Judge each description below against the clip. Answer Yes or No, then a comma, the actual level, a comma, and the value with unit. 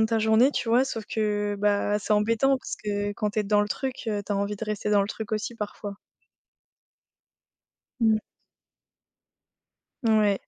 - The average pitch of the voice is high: Yes, high, 210 Hz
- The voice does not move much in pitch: Yes, narrow, 1.4 semitones